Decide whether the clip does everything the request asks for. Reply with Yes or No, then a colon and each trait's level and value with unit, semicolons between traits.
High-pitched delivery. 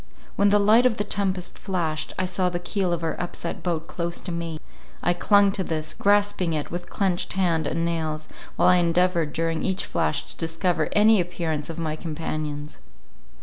No: medium, 175 Hz